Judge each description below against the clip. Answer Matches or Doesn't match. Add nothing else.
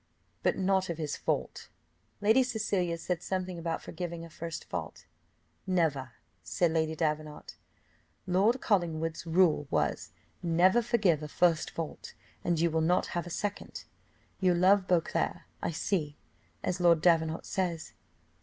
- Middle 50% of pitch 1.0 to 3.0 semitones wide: Matches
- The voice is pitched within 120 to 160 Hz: Doesn't match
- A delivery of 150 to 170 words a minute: Doesn't match